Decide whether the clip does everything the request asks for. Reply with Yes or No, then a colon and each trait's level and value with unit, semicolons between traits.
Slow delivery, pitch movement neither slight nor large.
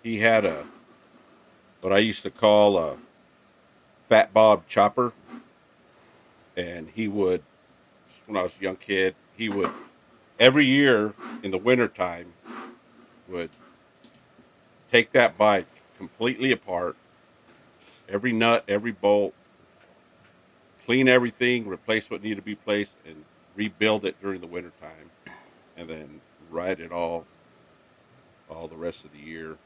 Yes: slow, 130 wpm; average, 4.7 semitones